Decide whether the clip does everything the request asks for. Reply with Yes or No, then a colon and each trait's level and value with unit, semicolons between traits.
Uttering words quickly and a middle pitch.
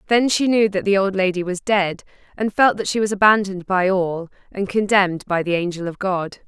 No: fast, 220 wpm; high, 195 Hz